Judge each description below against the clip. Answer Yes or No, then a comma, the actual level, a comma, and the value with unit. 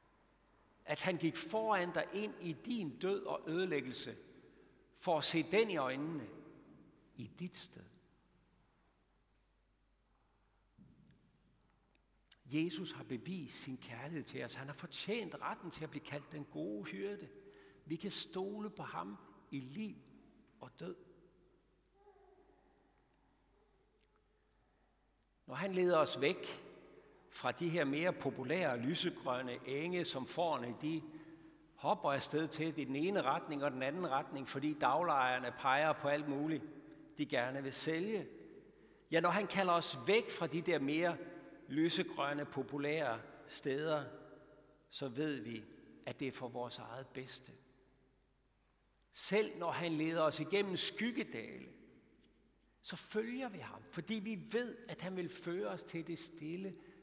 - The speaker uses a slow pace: Yes, slow, 135 wpm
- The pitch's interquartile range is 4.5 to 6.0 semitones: Yes, average, 4.8 semitones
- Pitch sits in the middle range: Yes, medium, 155 Hz